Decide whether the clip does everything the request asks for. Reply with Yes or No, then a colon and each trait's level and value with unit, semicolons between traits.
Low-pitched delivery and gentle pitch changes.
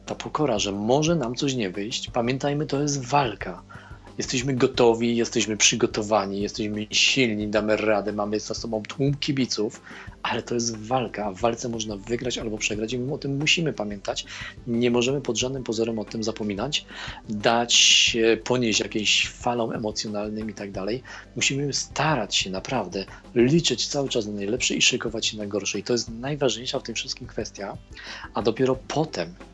No: low, 115 Hz; average, 3.3 semitones